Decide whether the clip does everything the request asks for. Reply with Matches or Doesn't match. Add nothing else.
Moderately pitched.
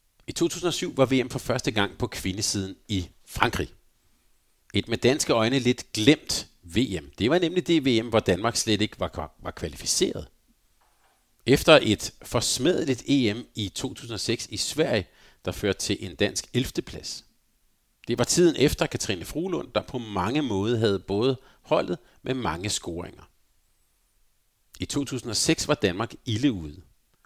Doesn't match